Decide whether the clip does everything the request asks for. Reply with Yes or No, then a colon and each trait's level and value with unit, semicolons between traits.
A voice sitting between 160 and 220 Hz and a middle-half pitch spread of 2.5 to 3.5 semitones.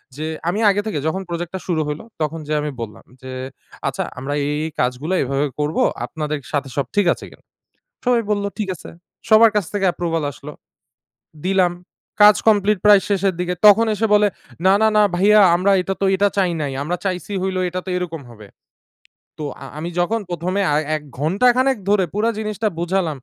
No: medium, 185 Hz; average, 5.0 semitones